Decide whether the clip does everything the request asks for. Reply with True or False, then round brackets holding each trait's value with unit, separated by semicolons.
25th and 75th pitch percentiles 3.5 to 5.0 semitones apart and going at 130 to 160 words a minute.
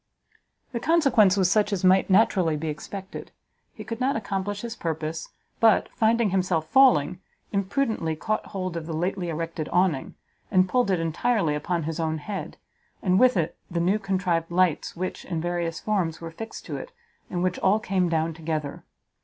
False (4.0 semitones; 175 wpm)